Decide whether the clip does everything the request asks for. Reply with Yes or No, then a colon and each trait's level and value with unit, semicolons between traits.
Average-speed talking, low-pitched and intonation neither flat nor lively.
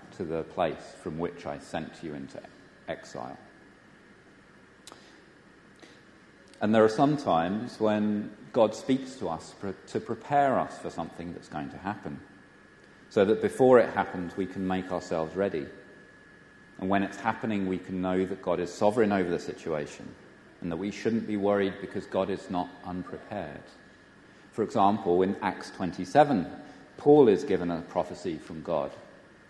Yes: average, 155 wpm; very low, 95 Hz; average, 3.0 semitones